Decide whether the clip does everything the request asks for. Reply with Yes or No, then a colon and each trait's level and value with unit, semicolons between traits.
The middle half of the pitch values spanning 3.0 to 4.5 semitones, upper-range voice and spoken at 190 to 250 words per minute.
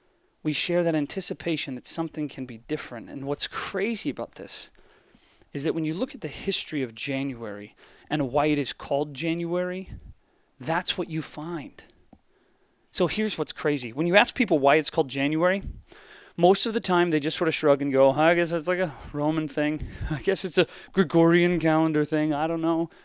No: average, 3.3 semitones; medium, 160 Hz; average, 195 wpm